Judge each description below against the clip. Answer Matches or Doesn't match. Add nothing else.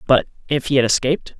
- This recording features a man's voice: Matches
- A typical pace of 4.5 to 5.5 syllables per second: Doesn't match